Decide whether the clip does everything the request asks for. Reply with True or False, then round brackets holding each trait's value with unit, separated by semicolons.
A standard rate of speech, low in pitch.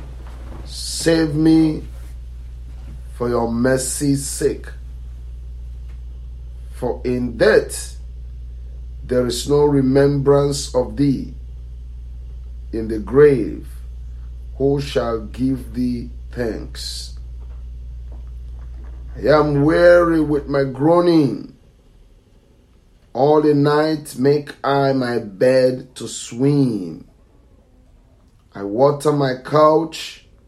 False (85 wpm; 115 Hz)